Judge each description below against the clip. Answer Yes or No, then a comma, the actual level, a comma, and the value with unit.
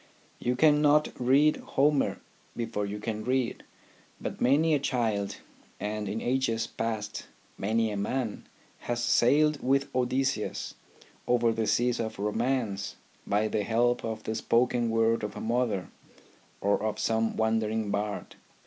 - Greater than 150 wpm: No, average, 140 wpm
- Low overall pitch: Yes, low, 115 Hz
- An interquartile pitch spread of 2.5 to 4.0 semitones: Yes, average, 2.9 semitones